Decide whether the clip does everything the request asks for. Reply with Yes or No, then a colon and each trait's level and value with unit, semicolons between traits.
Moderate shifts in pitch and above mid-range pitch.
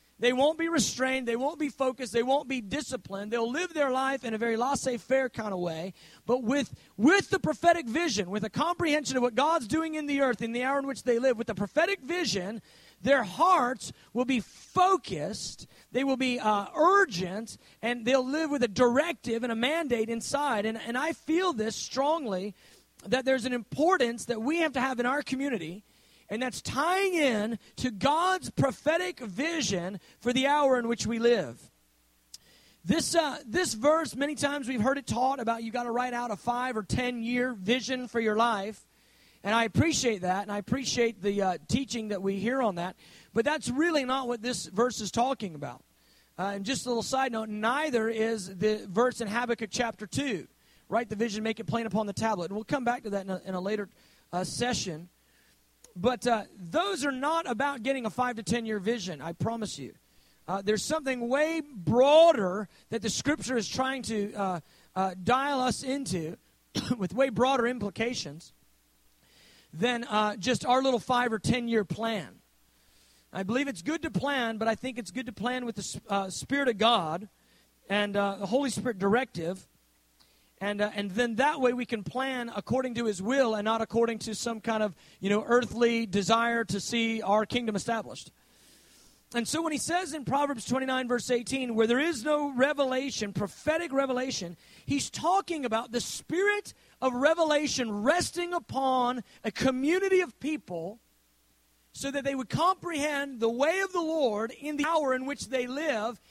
Yes: average, 4.5 semitones; high, 240 Hz